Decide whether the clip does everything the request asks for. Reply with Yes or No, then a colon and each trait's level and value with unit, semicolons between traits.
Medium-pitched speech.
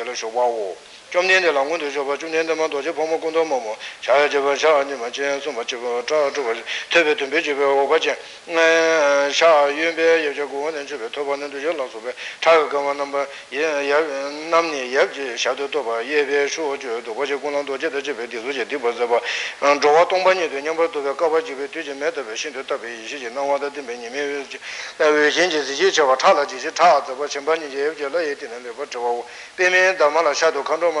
Yes: medium, 145 Hz